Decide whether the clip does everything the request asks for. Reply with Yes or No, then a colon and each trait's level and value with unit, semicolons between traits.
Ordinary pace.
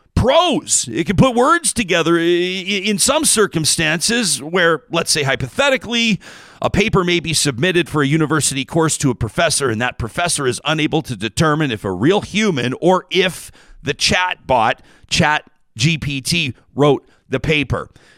Yes: average, 150 wpm